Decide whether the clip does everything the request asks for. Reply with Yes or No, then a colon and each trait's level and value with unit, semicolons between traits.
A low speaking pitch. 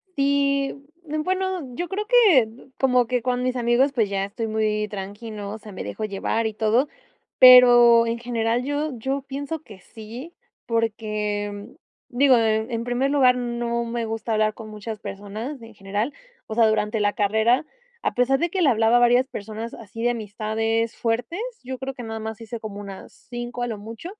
No: high, 230 Hz